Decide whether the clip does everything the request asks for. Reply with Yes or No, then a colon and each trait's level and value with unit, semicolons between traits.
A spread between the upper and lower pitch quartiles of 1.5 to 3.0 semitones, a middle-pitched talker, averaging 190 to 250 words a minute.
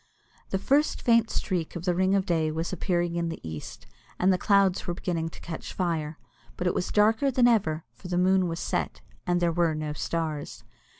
Yes: average, 2.7 semitones; medium, 175 Hz; fast, 205 wpm